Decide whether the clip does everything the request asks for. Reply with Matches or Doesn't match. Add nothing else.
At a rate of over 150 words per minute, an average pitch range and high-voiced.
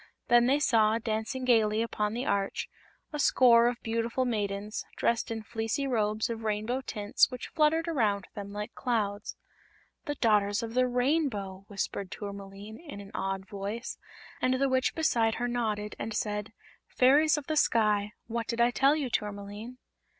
Matches